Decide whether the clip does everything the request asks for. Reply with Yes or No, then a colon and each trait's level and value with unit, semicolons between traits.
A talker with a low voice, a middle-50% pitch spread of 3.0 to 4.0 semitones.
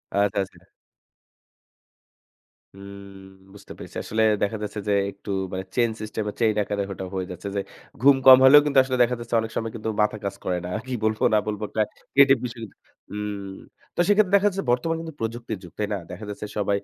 Yes: low, 105 Hz; average, 3.7 semitones